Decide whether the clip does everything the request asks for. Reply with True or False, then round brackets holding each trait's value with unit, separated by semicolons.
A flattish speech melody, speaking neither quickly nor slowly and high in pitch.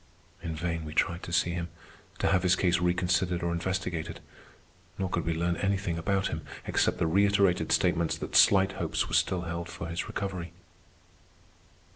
False (1.9 semitones; 170 wpm; 90 Hz)